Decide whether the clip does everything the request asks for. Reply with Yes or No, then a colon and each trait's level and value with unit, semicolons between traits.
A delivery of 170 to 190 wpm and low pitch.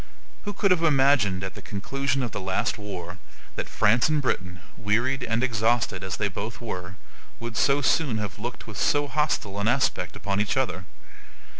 Yes: average, 180 wpm; low, 115 Hz